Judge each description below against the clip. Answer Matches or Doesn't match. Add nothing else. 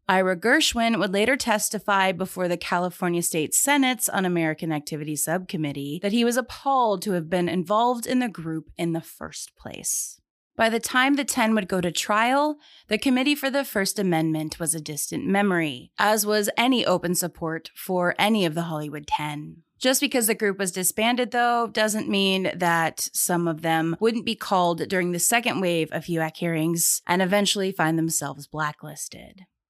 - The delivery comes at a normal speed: Matches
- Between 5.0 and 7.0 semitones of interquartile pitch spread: Matches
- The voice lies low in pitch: Doesn't match